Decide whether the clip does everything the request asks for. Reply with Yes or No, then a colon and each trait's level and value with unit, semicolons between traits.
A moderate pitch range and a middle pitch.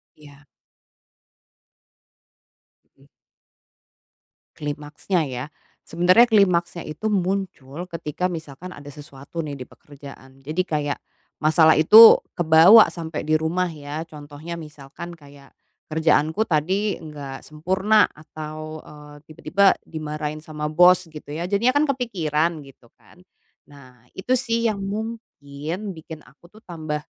Yes: average, 3.7 semitones; medium, 160 Hz